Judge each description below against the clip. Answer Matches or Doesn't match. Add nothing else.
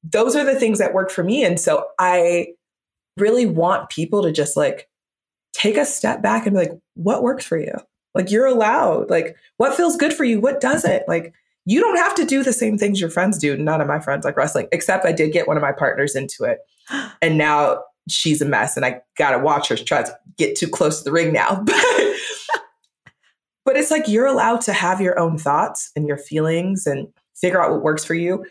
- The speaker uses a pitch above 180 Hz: Matches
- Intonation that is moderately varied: Doesn't match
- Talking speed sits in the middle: Doesn't match